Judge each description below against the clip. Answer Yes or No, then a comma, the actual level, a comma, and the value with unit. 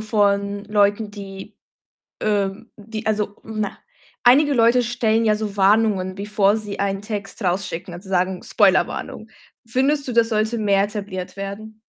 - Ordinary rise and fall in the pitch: No, narrow, 1.9 semitones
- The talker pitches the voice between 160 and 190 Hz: No, high, 210 Hz